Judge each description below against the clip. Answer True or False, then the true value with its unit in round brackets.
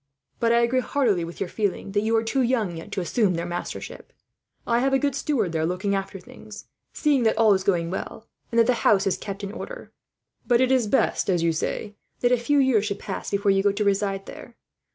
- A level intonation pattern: False (3.8 semitones)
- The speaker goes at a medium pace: False (235 wpm)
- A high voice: True (210 Hz)